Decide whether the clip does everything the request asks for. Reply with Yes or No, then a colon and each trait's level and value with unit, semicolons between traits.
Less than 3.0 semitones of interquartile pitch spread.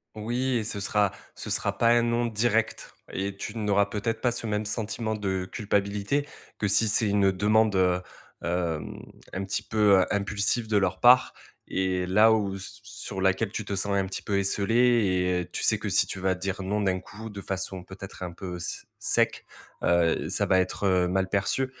Yes: narrow, 2.6 semitones